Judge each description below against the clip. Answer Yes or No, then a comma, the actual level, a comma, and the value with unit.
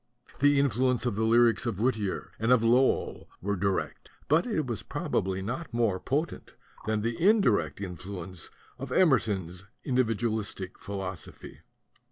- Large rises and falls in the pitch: No, average, 4.7 semitones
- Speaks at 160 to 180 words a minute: No, slow, 135 wpm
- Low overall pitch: Yes, low, 115 Hz